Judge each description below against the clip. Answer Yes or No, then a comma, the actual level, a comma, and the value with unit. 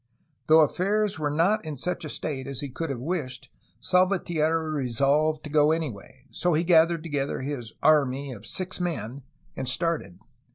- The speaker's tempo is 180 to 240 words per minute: No, average, 165 wpm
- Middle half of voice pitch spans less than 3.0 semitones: No, average, 3.5 semitones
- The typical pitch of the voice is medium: Yes, medium, 155 Hz